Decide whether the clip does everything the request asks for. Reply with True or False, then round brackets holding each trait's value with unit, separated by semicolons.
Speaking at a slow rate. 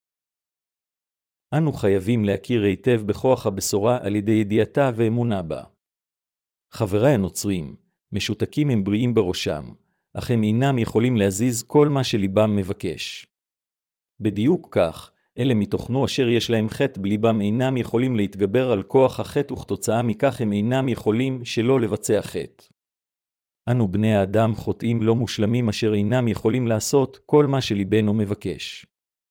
False (130 wpm)